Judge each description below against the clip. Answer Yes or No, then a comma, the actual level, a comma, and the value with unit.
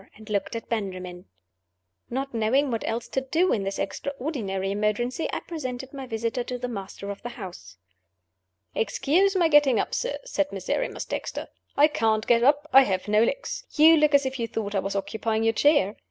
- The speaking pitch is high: Yes, high, 235 Hz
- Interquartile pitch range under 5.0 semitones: No, average, 5.3 semitones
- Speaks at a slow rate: No, average, 190 wpm